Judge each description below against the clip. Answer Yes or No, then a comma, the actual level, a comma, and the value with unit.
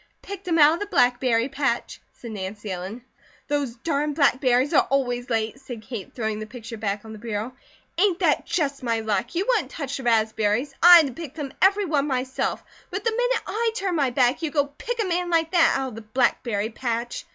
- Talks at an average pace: No, fast, 215 wpm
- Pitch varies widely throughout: Yes, wide, 6.3 semitones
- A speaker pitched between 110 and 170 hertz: No, very high, 265 Hz